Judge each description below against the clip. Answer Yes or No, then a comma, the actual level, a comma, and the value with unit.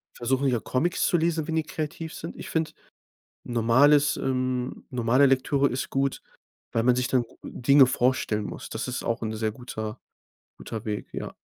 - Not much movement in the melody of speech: No, average, 3.5 semitones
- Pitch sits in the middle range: No, low, 130 Hz